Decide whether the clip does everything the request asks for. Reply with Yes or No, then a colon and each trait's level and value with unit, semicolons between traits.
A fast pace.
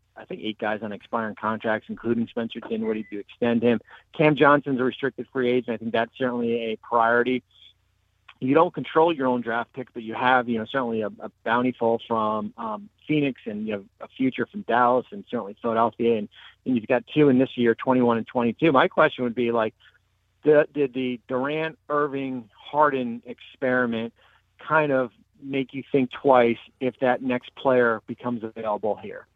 No: average, 185 wpm